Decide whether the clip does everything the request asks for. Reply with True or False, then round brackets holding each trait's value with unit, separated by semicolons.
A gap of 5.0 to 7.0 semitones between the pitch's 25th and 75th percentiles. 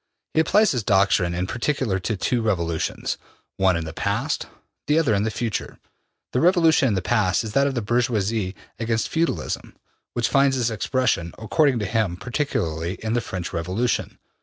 True (5.4 semitones)